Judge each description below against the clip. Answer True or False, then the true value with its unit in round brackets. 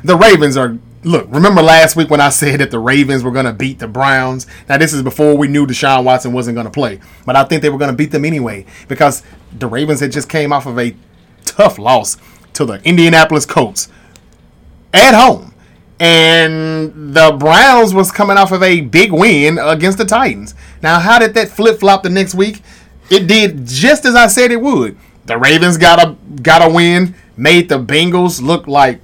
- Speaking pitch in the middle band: True (155 Hz)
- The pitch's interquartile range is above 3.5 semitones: True (4.9 semitones)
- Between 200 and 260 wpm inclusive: True (205 wpm)